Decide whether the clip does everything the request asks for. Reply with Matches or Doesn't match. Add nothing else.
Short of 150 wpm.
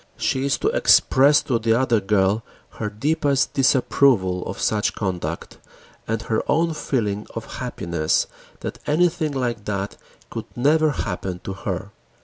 Matches